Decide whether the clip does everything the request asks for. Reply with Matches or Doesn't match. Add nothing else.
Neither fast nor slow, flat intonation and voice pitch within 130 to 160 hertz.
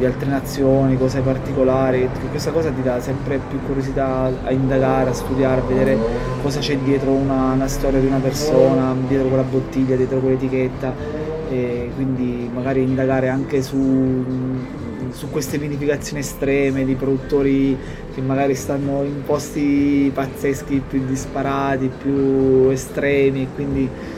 Matches